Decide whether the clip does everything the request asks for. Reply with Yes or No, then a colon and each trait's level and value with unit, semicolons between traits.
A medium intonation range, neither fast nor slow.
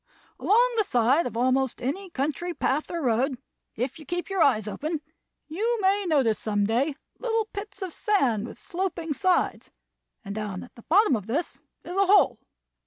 No: wide, 7.7 semitones; average, 175 wpm